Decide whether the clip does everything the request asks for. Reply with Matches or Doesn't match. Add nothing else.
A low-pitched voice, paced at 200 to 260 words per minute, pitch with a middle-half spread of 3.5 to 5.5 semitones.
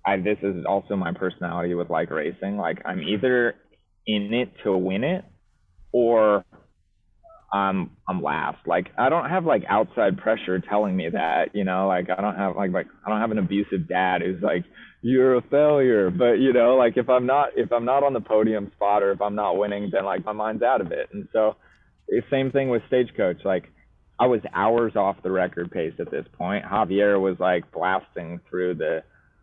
Matches